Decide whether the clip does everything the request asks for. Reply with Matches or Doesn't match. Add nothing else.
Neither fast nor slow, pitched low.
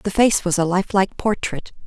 Doesn't match